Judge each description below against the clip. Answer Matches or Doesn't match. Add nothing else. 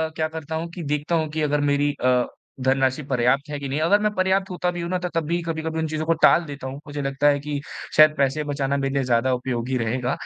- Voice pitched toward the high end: Doesn't match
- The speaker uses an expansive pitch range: Doesn't match